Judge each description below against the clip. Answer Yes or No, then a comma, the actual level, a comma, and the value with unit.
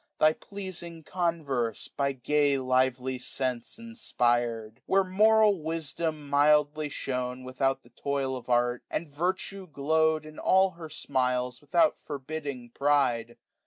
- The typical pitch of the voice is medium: Yes, medium, 145 Hz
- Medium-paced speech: No, slow, 125 wpm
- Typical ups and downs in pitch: Yes, average, 4.2 semitones